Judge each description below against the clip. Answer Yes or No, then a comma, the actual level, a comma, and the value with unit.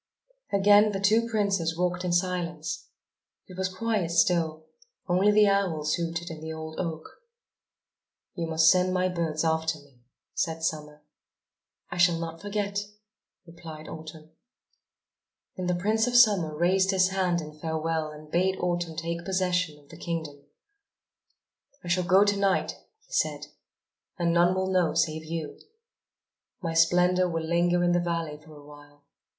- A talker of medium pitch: Yes, medium, 170 Hz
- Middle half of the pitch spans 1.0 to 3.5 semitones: Yes, narrow, 2.6 semitones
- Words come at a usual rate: Yes, average, 155 wpm